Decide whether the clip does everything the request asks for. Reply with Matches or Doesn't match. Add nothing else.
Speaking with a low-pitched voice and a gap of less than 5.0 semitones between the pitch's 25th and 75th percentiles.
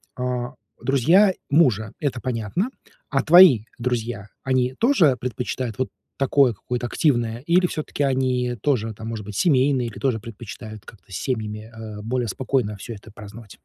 Matches